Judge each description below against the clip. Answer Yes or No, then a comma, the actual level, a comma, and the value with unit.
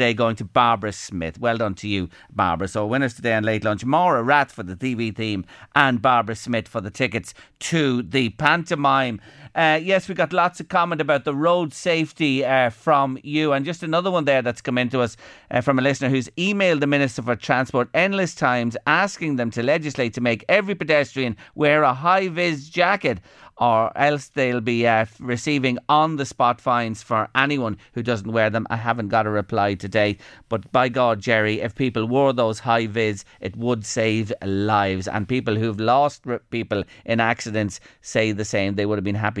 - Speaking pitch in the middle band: No, low, 120 Hz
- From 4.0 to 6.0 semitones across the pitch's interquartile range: Yes, average, 4.4 semitones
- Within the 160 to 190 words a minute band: No, average, 200 wpm